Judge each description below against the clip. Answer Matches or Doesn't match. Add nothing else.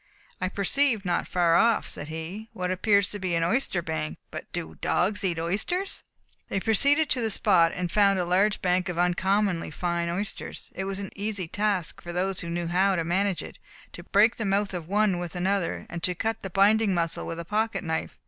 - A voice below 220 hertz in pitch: Matches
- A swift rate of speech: Matches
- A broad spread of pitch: Doesn't match